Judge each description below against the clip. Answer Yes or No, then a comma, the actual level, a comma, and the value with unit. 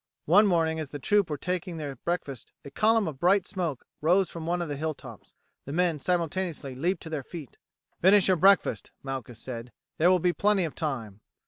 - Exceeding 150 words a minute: Yes, fast, 205 wpm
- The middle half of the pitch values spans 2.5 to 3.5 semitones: No, average, 4.4 semitones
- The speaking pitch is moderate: Yes, medium, 165 Hz